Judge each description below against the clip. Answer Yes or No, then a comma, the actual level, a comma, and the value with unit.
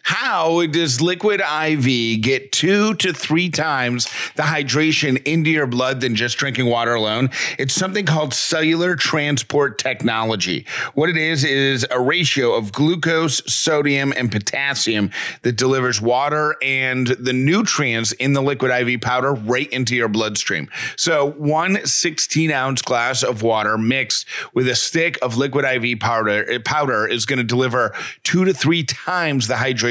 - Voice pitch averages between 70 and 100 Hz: No, low, 135 Hz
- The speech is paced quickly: No, average, 155 wpm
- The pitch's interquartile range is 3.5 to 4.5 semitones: Yes, average, 3.9 semitones